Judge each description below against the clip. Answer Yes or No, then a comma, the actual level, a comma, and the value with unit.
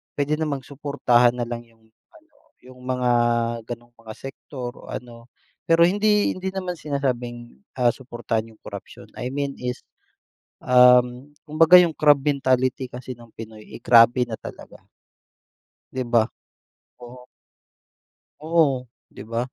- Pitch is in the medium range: No, low, 125 Hz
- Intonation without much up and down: No, average, 3.4 semitones